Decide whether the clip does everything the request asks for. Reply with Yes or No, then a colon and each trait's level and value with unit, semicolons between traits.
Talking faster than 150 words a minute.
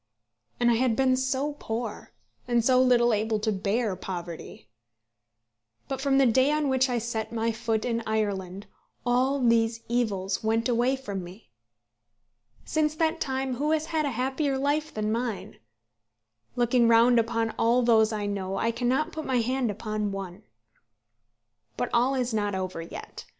Yes: average, 160 wpm